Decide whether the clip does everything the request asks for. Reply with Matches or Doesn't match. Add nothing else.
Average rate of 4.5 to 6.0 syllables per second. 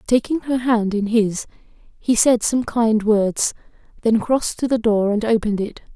Doesn't match